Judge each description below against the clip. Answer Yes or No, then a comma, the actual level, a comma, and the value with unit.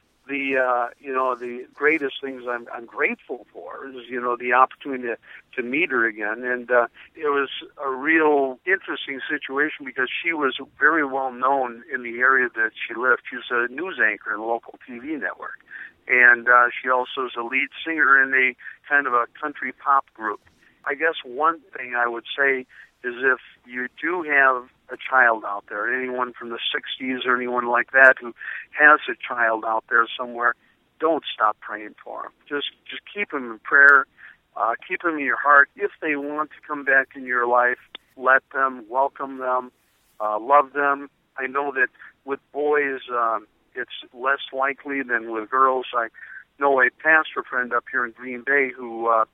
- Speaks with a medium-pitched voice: No, low, 130 Hz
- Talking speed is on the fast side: No, average, 185 wpm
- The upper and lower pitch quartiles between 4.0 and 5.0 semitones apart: No, narrow, 2.4 semitones